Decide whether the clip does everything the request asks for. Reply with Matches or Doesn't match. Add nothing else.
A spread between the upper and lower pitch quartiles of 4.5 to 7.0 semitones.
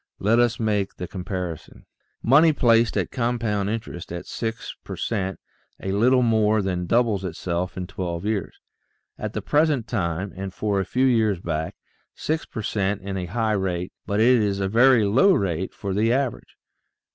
Doesn't match